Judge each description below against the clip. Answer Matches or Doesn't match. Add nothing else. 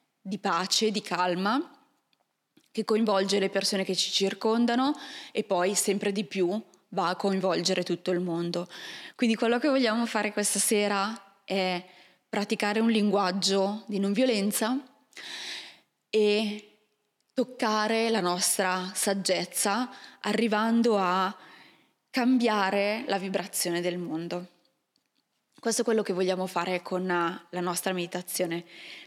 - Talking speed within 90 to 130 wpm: Matches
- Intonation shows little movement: Doesn't match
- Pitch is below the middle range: Doesn't match